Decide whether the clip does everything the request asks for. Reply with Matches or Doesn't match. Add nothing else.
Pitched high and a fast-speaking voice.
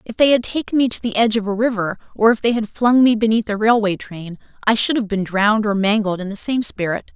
Matches